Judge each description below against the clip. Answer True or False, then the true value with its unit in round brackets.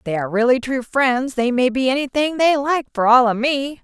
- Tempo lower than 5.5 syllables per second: True (5.3 syllables/s)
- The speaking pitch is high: True (255 Hz)